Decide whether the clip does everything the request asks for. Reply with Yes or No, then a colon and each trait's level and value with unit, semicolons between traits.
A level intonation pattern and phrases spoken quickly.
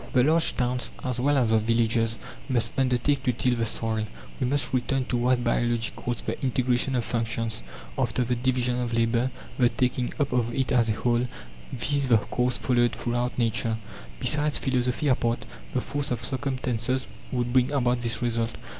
No: narrow, 1.6 semitones; average, 180 wpm